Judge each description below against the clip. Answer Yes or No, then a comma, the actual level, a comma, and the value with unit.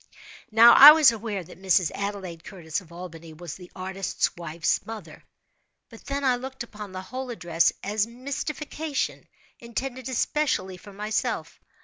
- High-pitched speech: Yes, high, 205 Hz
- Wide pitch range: Yes, wide, 5.9 semitones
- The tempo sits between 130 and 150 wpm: Yes, average, 145 wpm